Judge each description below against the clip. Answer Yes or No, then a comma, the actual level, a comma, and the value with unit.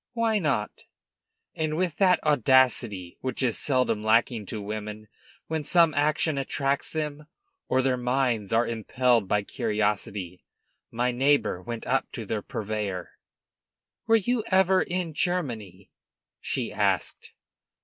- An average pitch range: No, wide, 6.0 semitones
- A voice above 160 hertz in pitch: No, low, 130 Hz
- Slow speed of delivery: Yes, slow, 130 wpm